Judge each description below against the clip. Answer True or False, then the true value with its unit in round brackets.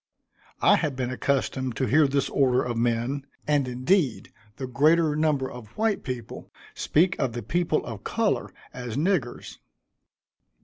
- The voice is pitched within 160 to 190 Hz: False (135 Hz)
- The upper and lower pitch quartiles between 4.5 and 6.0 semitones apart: False (3.7 semitones)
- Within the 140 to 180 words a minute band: True (145 wpm)